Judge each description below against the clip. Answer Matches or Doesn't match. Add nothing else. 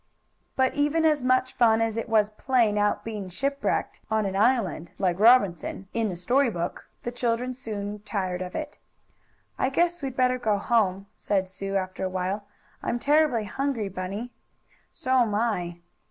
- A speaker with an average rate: Matches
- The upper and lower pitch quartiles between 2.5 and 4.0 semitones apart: Doesn't match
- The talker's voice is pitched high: Matches